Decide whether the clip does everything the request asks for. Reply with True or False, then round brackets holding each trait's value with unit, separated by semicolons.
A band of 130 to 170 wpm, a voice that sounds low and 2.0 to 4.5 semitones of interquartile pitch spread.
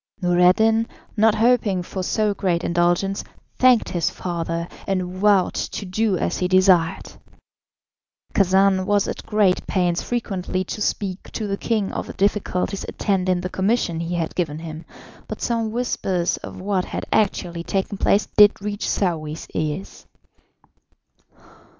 False (140 wpm; 190 Hz; 2.9 semitones)